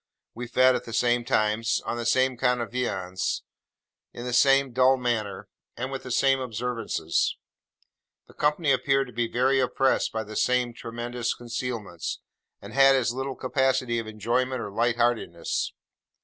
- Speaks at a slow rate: No, average, 160 wpm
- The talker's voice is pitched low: Yes, low, 120 Hz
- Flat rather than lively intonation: Yes, narrow, 2.0 semitones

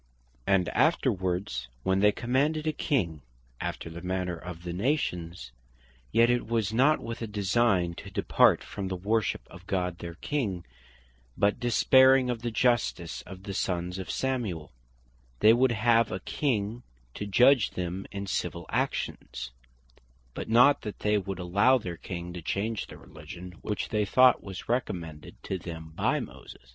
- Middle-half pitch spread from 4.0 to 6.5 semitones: Yes, average, 5.1 semitones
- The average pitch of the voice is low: Yes, low, 100 Hz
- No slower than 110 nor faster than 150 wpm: No, average, 160 wpm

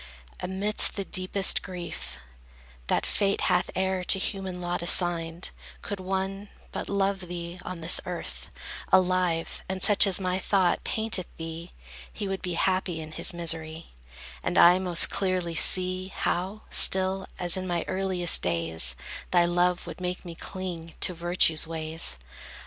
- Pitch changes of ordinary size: No, narrow, 1.9 semitones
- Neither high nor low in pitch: Yes, medium, 180 Hz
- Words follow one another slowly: No, average, 150 wpm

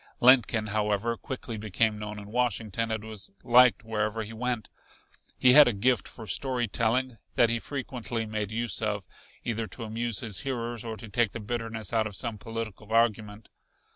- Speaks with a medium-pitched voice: No, low, 115 Hz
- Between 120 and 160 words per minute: No, average, 175 wpm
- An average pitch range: No, narrow, 1.9 semitones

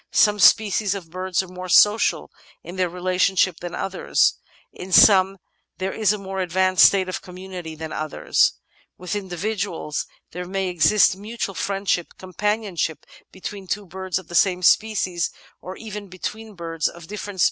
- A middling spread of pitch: No, narrow, 2.1 semitones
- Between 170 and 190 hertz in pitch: Yes, medium, 185 Hz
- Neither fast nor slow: Yes, average, 170 wpm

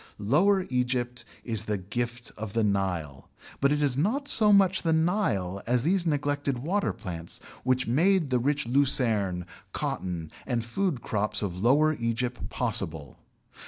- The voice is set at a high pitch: No, low, 125 Hz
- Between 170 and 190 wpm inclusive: No, average, 150 wpm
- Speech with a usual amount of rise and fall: No, wide, 6.4 semitones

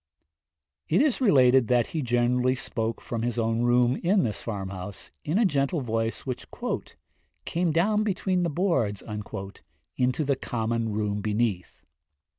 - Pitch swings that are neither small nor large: No, wide, 6.3 semitones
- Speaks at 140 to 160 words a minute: Yes, average, 145 wpm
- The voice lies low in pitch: Yes, low, 125 Hz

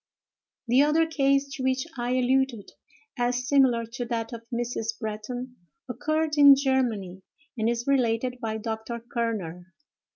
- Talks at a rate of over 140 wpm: No, slow, 135 wpm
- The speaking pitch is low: No, high, 245 Hz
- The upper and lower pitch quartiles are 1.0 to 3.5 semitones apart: Yes, average, 2.7 semitones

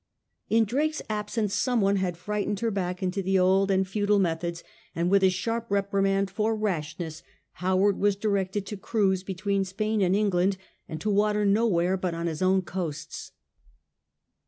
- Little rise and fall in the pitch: Yes, narrow, 2.3 semitones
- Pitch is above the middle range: Yes, high, 195 Hz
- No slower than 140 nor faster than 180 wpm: Yes, average, 165 wpm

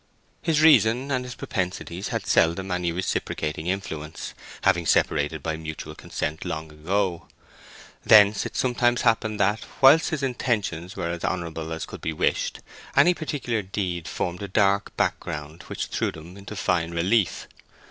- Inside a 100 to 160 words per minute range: Yes, average, 150 wpm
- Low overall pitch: Yes, very low, 95 Hz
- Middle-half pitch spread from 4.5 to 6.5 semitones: Yes, average, 5.3 semitones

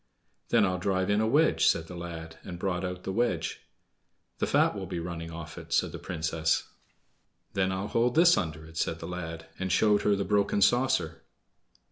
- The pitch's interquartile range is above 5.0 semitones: No, average, 3.7 semitones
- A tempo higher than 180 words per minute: Yes, average, 195 wpm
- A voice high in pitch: No, very low, 90 Hz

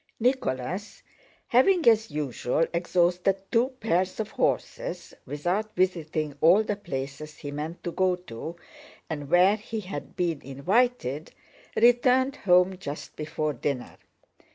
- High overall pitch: No, medium, 180 Hz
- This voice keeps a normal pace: No, slow, 125 wpm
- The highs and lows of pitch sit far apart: Yes, wide, 6.1 semitones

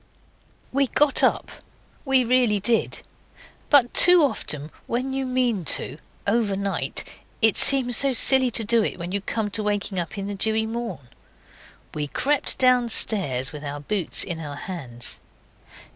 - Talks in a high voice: Yes, high, 220 Hz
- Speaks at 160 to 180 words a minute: No, average, 145 wpm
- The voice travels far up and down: Yes, wide, 5.8 semitones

